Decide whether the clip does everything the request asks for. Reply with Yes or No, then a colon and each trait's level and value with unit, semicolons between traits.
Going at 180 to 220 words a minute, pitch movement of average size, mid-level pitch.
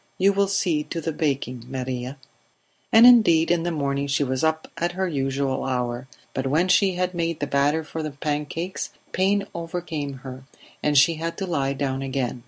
Yes: average, 190 wpm; average, 4.2 semitones; medium, 150 Hz